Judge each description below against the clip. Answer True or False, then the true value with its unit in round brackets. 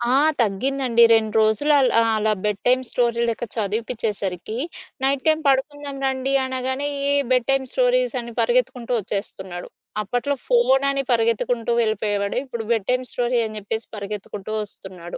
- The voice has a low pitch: False (235 Hz)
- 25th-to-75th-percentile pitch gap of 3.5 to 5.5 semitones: True (3.9 semitones)